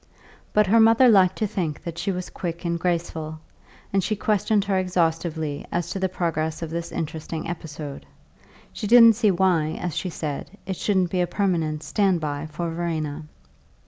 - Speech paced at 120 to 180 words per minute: Yes, average, 175 wpm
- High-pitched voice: No, medium, 175 Hz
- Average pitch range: Yes, average, 3.3 semitones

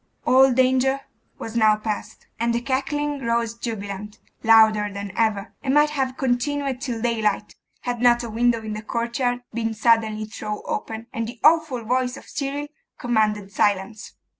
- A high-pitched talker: Yes, high, 235 Hz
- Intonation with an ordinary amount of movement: Yes, average, 3.1 semitones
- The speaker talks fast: No, average, 160 wpm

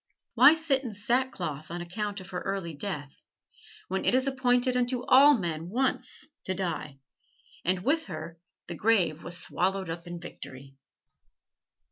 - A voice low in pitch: No, high, 190 Hz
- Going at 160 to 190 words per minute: No, average, 150 wpm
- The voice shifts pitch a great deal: Yes, wide, 6.6 semitones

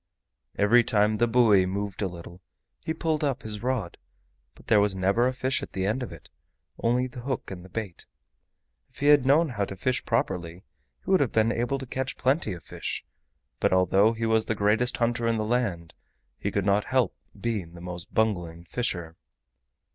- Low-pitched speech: Yes, low, 110 Hz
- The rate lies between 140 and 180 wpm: No, average, 200 wpm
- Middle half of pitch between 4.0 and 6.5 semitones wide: Yes, average, 4.6 semitones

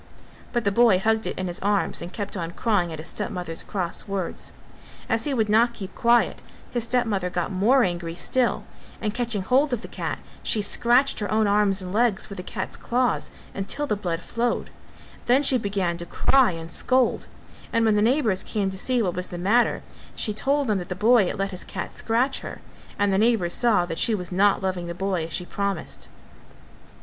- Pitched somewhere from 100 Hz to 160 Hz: No, high, 205 Hz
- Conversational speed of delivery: No, fast, 210 wpm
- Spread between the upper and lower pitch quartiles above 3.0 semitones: Yes, average, 4.4 semitones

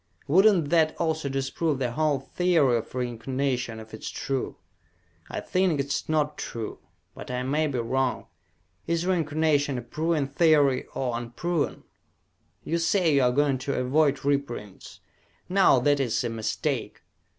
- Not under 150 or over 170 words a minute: Yes, average, 155 wpm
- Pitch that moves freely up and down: No, average, 3.8 semitones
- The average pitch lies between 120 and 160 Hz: Yes, medium, 140 Hz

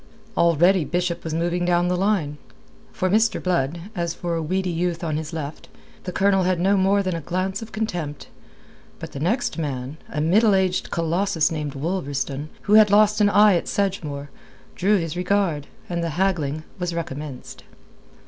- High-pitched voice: No, medium, 175 Hz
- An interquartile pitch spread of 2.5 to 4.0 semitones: Yes, average, 3.5 semitones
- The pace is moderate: Yes, average, 175 wpm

